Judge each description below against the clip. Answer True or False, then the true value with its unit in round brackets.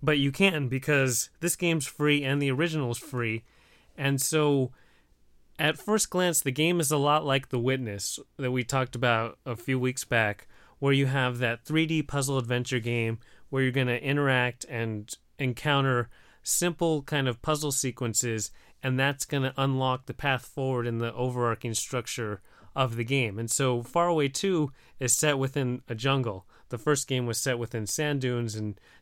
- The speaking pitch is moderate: False (130 Hz)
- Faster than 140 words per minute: True (180 wpm)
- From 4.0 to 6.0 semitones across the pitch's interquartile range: False (3.2 semitones)